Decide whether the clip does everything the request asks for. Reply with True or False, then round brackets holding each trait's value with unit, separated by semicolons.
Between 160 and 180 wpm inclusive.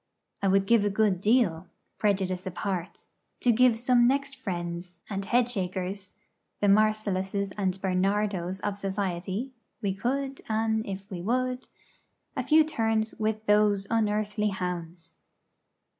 False (135 wpm)